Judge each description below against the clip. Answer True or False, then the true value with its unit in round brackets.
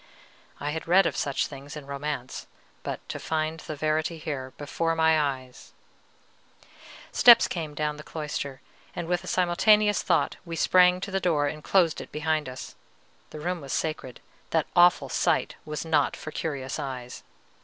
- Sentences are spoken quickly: False (165 wpm)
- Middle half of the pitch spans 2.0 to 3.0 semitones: True (2.7 semitones)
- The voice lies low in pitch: False (155 Hz)